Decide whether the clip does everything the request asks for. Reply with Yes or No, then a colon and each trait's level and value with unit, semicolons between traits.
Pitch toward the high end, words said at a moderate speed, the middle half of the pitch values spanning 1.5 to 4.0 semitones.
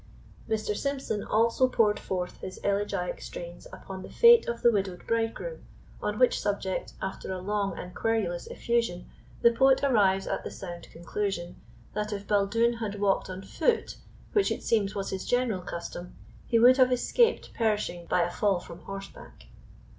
Yes: high, 205 Hz; average, 165 wpm; average, 3.7 semitones